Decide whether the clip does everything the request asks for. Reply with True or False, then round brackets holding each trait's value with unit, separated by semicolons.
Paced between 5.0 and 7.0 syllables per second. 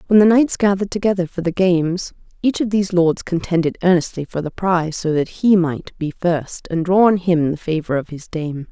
True (5.4 syllables/s)